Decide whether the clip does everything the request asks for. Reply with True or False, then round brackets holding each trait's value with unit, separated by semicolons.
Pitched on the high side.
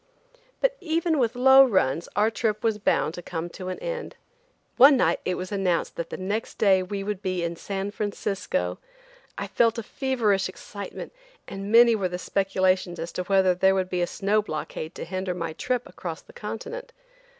True (195 Hz)